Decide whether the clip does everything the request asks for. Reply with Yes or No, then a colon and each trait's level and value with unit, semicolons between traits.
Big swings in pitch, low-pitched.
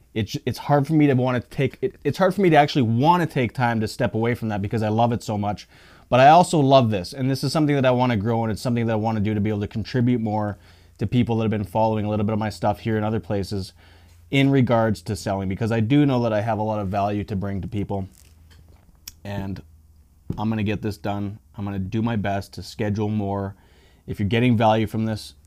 No: average, 3.3 semitones; low, 110 Hz